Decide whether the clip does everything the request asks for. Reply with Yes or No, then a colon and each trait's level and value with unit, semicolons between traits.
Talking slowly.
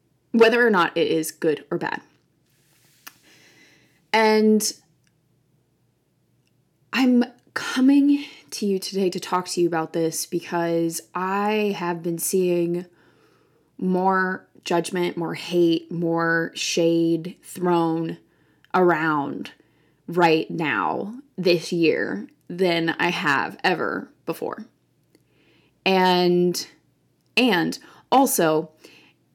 Yes: slow, 90 wpm